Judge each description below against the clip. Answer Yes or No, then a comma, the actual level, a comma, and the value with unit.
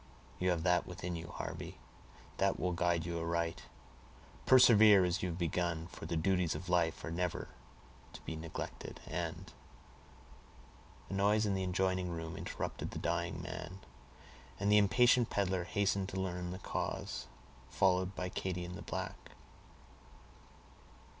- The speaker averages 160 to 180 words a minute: No, average, 145 wpm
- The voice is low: Yes, very low, 90 Hz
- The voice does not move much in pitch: Yes, narrow, 2.0 semitones